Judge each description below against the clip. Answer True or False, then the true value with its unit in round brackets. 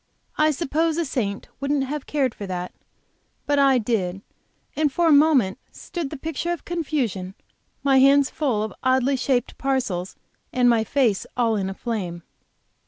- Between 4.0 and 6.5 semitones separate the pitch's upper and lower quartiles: True (5.3 semitones)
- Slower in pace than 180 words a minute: True (165 wpm)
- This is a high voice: True (265 Hz)